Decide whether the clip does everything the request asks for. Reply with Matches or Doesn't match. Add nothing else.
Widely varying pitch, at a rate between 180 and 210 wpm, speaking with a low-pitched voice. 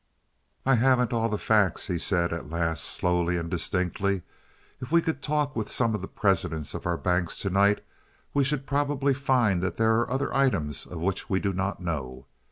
Matches